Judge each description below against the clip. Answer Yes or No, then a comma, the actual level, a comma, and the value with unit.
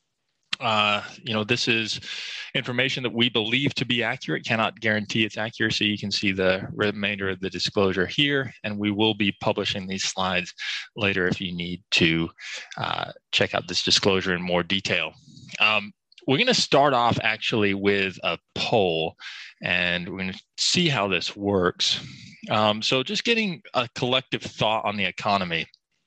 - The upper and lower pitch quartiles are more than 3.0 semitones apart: Yes, average, 4.0 semitones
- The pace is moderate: Yes, average, 170 wpm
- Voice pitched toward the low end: Yes, low, 105 Hz